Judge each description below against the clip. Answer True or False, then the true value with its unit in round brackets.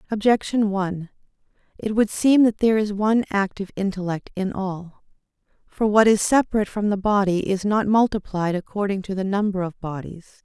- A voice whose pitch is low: False (200 Hz)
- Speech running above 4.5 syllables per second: True (5.6 syllables/s)